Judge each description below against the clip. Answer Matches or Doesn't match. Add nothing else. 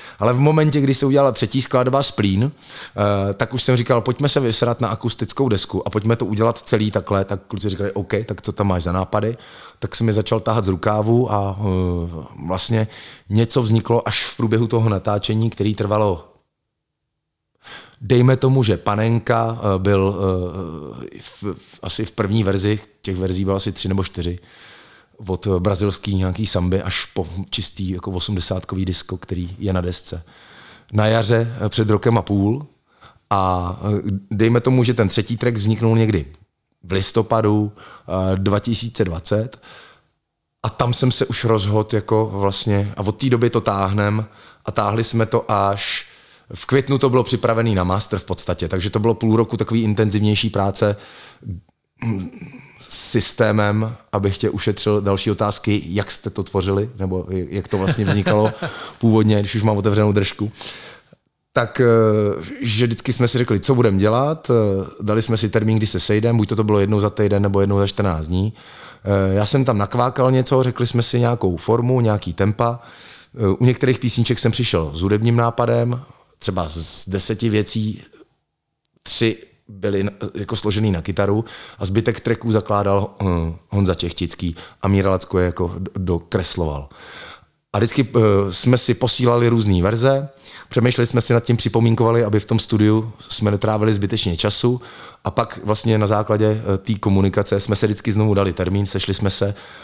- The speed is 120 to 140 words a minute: Doesn't match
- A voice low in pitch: Matches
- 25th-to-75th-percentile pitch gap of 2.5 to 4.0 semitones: Matches